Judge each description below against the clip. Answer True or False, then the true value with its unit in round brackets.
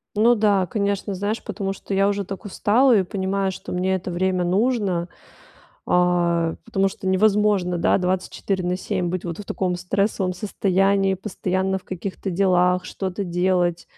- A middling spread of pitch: False (1.9 semitones)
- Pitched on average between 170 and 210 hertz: True (190 Hz)